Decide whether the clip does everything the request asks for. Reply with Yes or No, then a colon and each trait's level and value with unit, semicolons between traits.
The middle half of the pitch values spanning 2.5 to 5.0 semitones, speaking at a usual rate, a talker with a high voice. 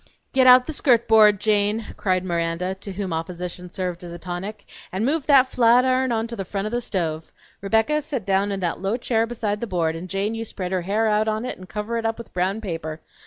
No: average, 4.0 semitones; fast, 240 wpm; high, 205 Hz